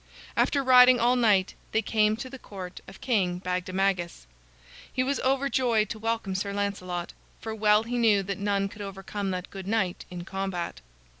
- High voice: Yes, high, 205 Hz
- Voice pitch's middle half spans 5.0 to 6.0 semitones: No, average, 3.3 semitones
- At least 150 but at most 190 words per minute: Yes, average, 170 wpm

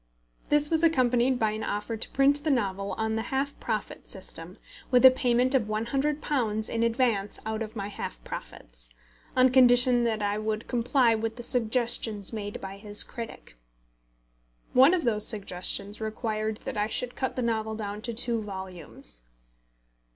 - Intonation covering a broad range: No, average, 3.2 semitones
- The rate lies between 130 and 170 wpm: Yes, average, 165 wpm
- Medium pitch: No, high, 225 Hz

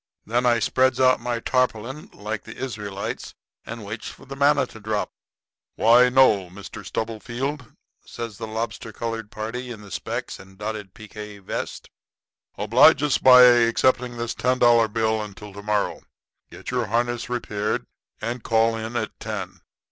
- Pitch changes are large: No, narrow, 2.6 semitones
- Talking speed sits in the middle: Yes, average, 155 wpm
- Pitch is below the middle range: Yes, low, 115 Hz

